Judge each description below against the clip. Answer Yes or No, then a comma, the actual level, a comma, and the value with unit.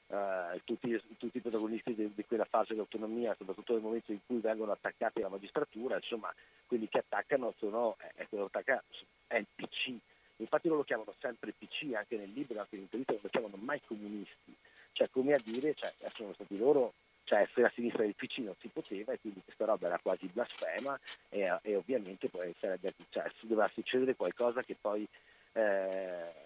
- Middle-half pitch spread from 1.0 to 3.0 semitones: Yes, average, 2.7 semitones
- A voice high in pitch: No, low, 115 Hz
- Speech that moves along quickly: Yes, fast, 190 wpm